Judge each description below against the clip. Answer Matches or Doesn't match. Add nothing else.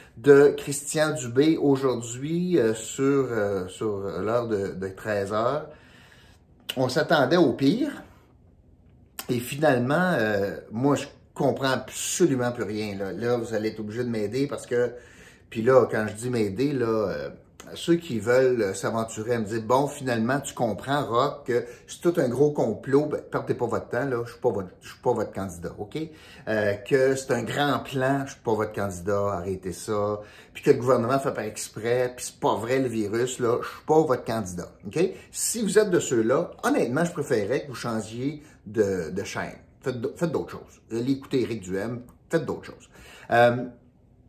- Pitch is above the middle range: Doesn't match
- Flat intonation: Doesn't match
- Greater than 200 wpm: Doesn't match